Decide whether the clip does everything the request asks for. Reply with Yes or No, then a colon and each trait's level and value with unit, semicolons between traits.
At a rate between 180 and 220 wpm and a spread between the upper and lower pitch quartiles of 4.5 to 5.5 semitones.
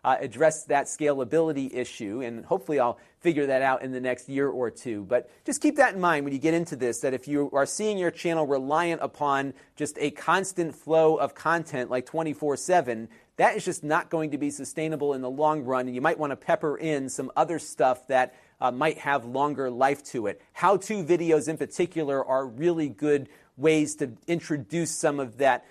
No: fast, 205 wpm; average, 3.2 semitones